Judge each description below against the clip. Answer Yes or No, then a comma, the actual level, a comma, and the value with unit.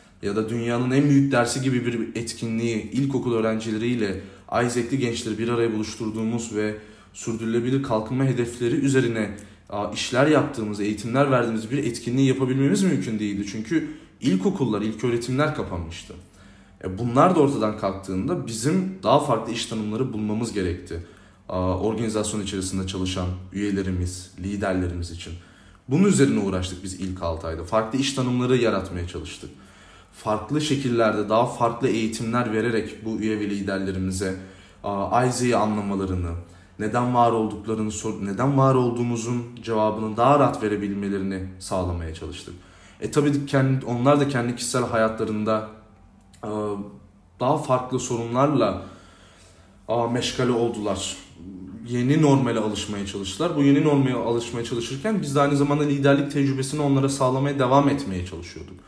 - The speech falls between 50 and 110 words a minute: No, average, 125 wpm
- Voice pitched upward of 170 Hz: No, low, 110 Hz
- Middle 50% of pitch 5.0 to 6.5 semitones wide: No, average, 4.3 semitones